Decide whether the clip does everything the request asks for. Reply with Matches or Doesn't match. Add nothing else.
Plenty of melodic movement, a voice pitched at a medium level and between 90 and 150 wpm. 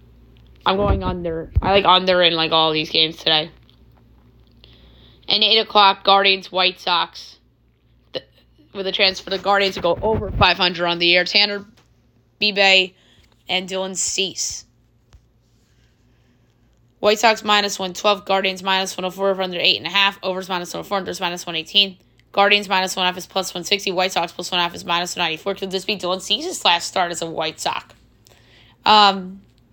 Doesn't match